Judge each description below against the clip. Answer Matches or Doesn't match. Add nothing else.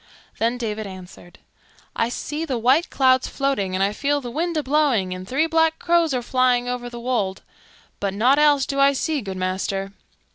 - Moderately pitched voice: Doesn't match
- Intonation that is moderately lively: Doesn't match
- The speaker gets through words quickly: Doesn't match